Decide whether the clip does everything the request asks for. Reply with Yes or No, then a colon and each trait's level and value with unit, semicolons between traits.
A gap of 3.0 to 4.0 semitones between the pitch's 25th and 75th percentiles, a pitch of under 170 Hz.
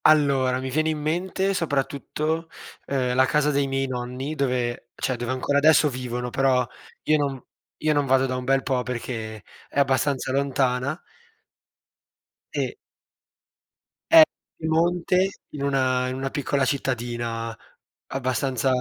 No: narrow, 2.6 semitones; low, 135 Hz